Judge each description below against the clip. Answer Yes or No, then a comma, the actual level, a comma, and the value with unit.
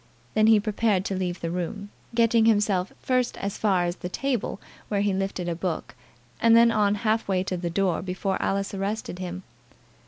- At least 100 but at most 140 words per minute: No, average, 190 wpm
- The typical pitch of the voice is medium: No, high, 195 Hz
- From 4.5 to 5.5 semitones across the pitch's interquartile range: No, average, 2.9 semitones